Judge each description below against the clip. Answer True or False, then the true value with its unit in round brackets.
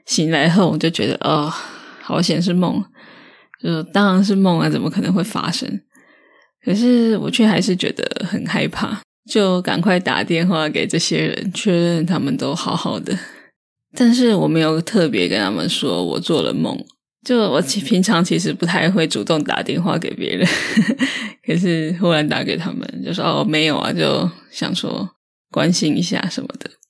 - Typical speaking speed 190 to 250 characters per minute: True (245 characters per minute)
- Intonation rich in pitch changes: False (4.7 semitones)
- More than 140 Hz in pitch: True (185 Hz)